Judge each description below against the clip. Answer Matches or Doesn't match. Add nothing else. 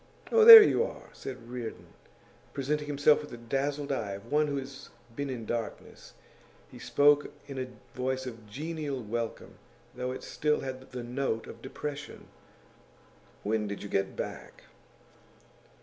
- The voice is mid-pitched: Doesn't match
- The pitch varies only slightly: Doesn't match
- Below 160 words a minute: Matches